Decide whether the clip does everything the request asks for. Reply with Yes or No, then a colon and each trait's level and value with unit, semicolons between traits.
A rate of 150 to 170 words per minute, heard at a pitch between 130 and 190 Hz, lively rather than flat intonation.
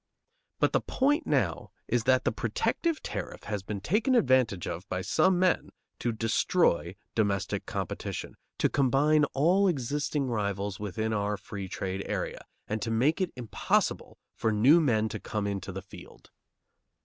No: average, 155 wpm; low, 115 Hz; wide, 6.7 semitones